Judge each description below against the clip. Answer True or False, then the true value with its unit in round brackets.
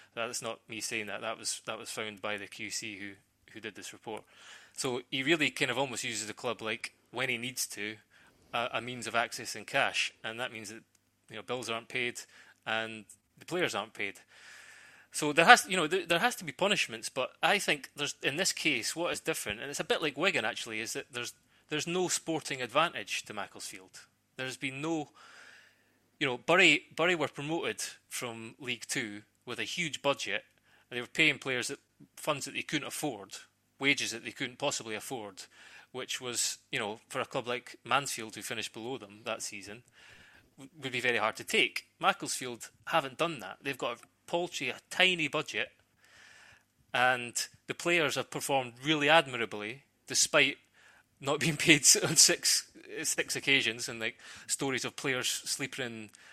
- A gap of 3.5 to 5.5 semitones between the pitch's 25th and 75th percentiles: True (4.1 semitones)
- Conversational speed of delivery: True (190 wpm)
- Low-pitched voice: True (125 Hz)